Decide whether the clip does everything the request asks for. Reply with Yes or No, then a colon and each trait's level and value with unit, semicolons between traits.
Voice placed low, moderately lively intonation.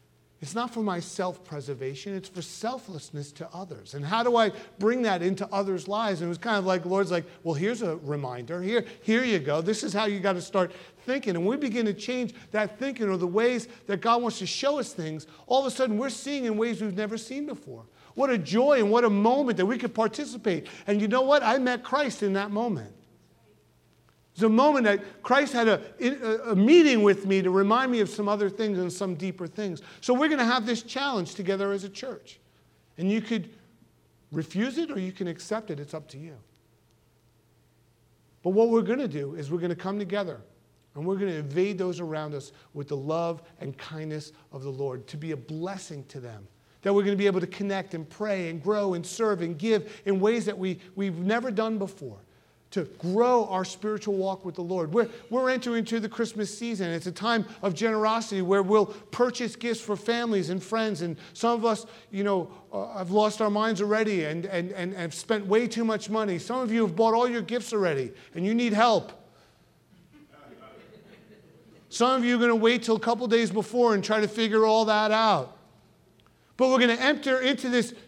No: high, 205 Hz; average, 4.5 semitones